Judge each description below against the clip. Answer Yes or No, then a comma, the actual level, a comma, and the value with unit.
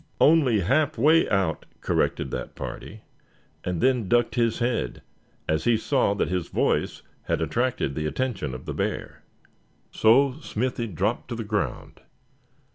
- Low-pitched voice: Yes, low, 115 Hz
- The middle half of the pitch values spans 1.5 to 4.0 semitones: No, wide, 5.4 semitones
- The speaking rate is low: No, average, 145 wpm